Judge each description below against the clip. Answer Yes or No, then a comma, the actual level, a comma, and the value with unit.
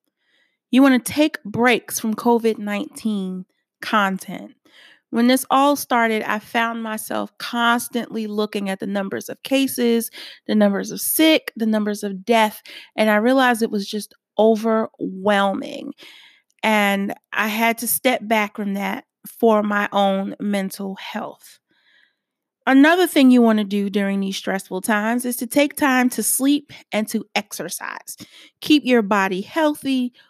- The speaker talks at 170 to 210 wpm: No, average, 145 wpm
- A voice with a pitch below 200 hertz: No, high, 225 Hz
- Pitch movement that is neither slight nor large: Yes, average, 4.2 semitones